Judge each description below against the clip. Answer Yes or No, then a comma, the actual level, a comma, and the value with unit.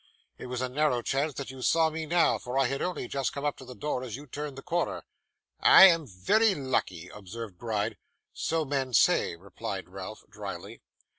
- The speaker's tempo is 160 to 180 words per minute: No, average, 200 wpm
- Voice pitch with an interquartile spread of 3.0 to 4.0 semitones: No, average, 4.4 semitones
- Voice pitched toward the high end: No, low, 135 Hz